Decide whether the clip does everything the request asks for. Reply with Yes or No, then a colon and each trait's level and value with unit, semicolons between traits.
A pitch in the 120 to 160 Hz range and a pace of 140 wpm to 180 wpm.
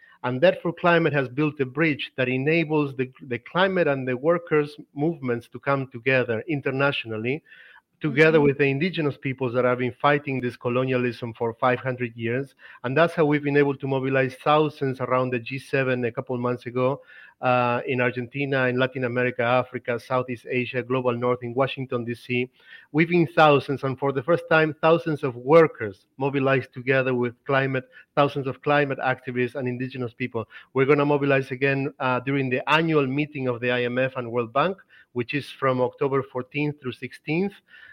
Yes: low, 135 Hz; average, 175 wpm